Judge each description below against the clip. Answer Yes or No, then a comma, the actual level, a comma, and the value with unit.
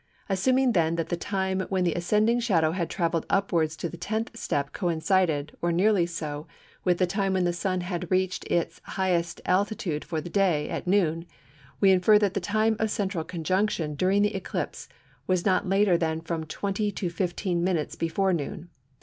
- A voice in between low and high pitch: Yes, medium, 180 Hz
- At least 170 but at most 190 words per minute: Yes, average, 185 wpm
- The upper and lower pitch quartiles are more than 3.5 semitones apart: No, average, 2.9 semitones